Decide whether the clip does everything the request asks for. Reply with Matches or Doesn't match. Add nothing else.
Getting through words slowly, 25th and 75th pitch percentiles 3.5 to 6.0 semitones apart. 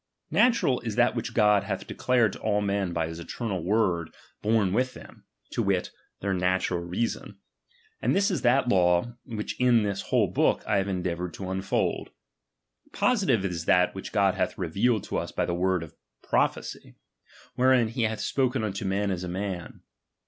Doesn't match